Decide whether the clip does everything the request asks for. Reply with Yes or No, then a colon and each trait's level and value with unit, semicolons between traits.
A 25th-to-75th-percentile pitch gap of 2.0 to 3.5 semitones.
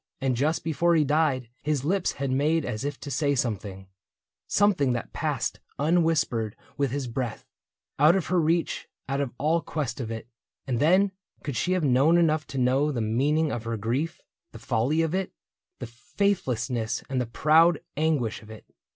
No: average, 4.8 semitones